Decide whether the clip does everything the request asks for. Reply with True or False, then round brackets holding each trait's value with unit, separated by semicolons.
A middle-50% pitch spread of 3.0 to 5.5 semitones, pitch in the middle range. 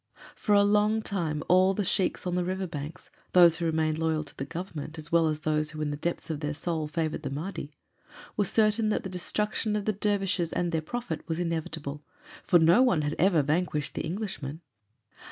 True (4.0 semitones; 170 Hz)